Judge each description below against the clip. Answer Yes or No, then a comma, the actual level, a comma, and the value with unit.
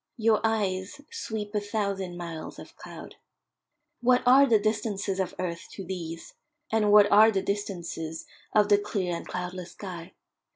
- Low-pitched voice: No, high, 200 Hz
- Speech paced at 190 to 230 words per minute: No, average, 155 wpm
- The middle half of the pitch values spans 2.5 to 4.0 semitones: Yes, average, 3.1 semitones